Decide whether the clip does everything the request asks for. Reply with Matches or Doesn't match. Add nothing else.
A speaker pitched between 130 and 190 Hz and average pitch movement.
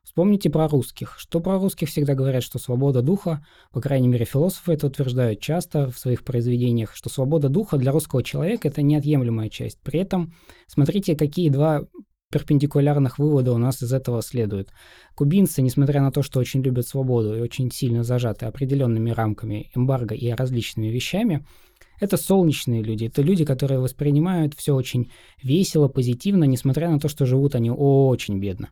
Matches